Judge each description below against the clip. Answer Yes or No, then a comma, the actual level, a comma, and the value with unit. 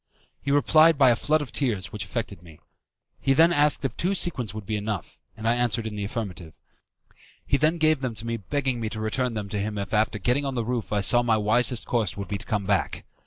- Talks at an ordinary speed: No, fast, 245 wpm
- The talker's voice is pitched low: Yes, low, 115 Hz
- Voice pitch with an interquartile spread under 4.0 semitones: No, average, 4.5 semitones